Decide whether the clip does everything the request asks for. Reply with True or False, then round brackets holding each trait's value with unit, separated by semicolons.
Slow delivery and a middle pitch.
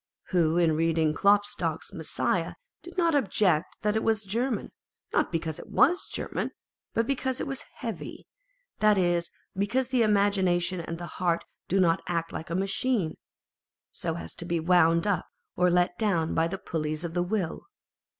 False (170 wpm; 180 Hz)